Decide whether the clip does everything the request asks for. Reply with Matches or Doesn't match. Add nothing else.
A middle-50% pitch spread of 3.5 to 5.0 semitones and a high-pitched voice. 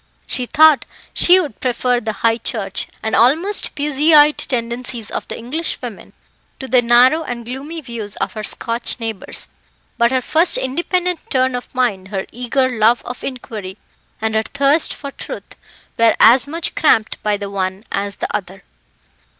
Matches